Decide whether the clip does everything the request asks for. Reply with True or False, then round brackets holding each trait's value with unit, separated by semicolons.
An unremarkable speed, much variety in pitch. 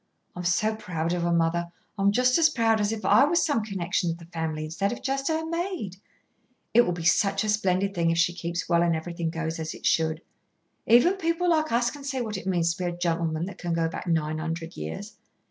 False (230 wpm; 5.8 semitones)